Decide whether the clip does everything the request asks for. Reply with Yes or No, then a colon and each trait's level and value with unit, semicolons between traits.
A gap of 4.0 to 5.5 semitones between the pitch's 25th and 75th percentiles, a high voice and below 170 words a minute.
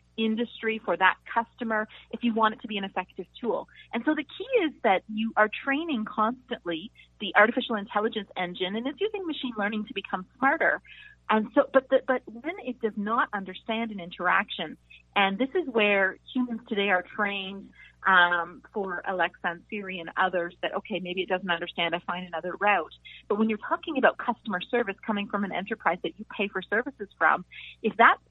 No: average, 4.4 semitones; high, 215 Hz; average, 195 wpm